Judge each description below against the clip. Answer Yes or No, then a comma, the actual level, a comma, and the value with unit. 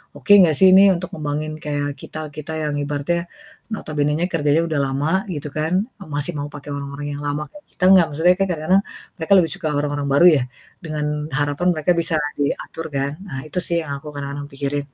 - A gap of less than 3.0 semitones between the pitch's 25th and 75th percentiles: Yes, narrow, 2.4 semitones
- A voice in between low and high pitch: Yes, medium, 150 Hz